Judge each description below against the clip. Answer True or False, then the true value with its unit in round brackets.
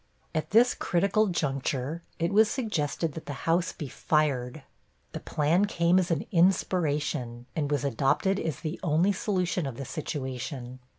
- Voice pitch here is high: False (155 Hz)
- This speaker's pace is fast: False (155 wpm)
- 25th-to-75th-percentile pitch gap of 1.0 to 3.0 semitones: False (4.5 semitones)